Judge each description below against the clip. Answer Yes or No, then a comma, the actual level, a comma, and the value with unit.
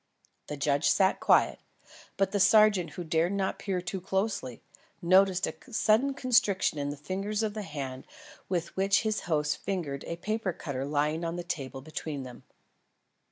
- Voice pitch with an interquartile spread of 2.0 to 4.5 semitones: No, average, 5.0 semitones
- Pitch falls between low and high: Yes, medium, 175 Hz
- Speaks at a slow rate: No, average, 165 wpm